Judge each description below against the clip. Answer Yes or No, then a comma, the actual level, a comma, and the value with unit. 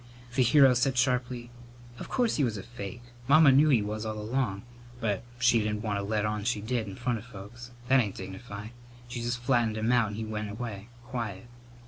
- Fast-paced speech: Yes, fast, 210 wpm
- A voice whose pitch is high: No, low, 115 Hz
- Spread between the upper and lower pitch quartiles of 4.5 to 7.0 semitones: No, average, 2.8 semitones